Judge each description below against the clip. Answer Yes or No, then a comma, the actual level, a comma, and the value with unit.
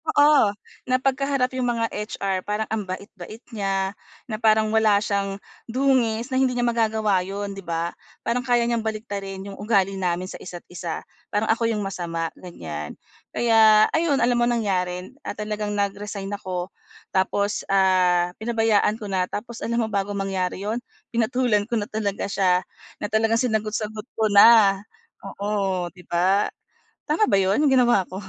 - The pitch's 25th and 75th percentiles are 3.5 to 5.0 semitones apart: No, average, 3.0 semitones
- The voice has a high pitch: Yes, high, 210 Hz